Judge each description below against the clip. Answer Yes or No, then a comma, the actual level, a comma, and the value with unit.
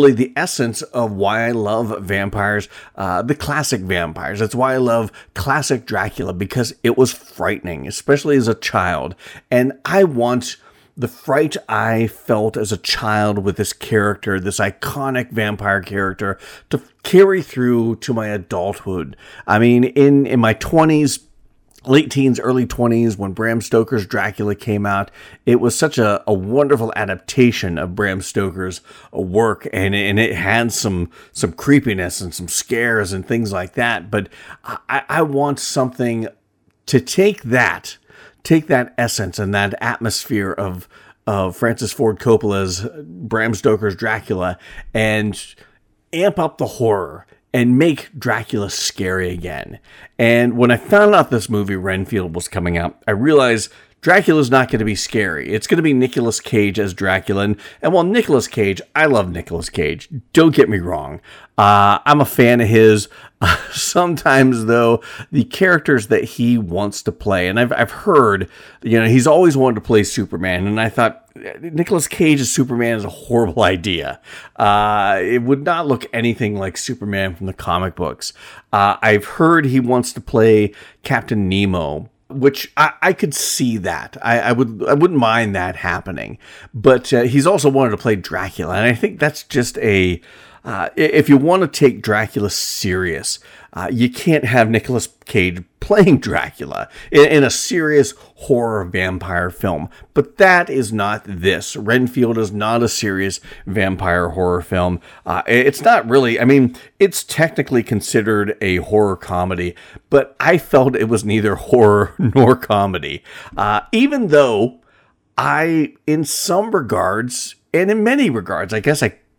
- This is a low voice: Yes, low, 115 Hz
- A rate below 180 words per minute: Yes, average, 160 wpm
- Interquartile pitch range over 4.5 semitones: Yes, average, 4.9 semitones